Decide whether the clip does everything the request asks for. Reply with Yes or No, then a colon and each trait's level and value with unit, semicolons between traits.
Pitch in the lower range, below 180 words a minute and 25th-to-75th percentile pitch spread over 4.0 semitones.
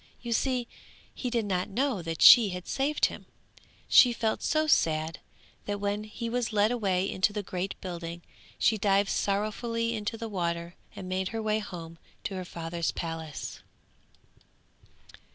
No: high, 200 Hz; average, 155 wpm; average, 4.5 semitones